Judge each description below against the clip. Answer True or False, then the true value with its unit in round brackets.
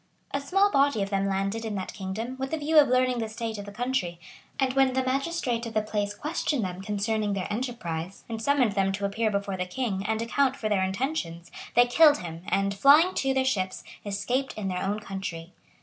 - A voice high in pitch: True (220 Hz)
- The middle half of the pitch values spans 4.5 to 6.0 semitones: True (5.0 semitones)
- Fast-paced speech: True (215 wpm)